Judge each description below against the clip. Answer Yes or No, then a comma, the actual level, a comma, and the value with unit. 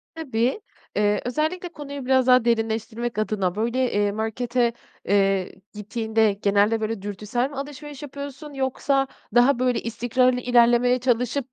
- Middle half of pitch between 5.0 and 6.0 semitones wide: No, average, 3.2 semitones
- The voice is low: No, high, 240 Hz